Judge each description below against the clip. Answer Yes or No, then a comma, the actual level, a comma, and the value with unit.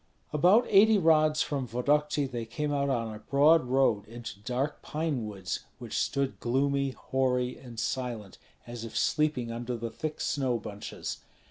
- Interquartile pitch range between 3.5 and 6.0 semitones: Yes, average, 4.2 semitones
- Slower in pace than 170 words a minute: Yes, average, 155 wpm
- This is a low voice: Yes, low, 130 Hz